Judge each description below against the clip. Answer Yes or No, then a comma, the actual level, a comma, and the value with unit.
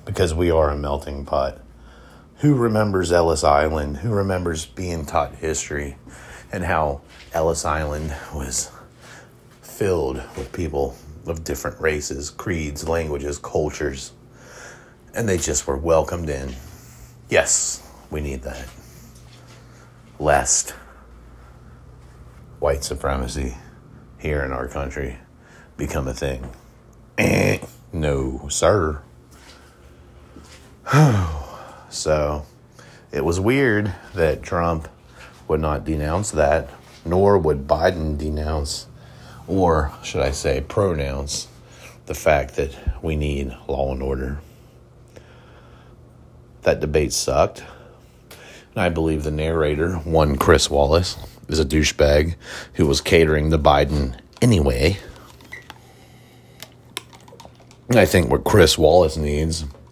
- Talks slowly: Yes, slow, 105 wpm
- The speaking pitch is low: Yes, very low, 75 Hz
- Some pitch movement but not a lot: Yes, average, 3.3 semitones